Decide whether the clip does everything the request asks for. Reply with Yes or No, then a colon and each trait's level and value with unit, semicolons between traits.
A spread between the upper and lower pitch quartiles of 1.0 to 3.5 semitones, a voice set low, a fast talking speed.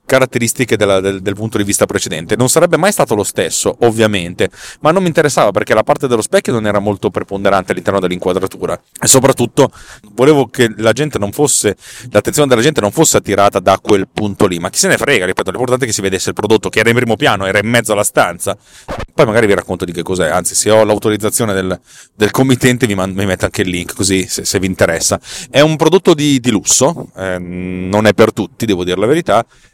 No: average, 4.8 semitones; low, 105 Hz; fast, 225 wpm